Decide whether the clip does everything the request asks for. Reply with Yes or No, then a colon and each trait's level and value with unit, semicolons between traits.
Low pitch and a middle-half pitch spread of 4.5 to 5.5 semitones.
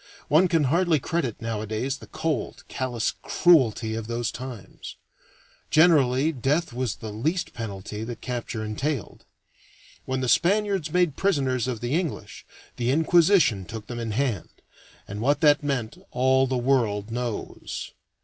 Yes: low, 130 Hz; average, 5.2 semitones